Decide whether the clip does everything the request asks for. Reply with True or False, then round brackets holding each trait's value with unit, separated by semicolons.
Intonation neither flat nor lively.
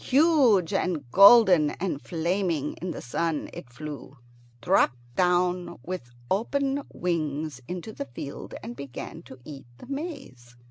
False (5.7 semitones)